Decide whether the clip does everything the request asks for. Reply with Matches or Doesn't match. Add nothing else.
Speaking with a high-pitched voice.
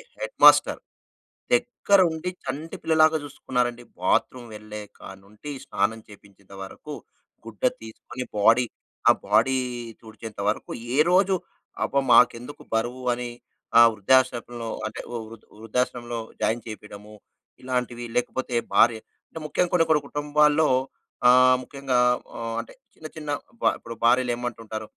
Doesn't match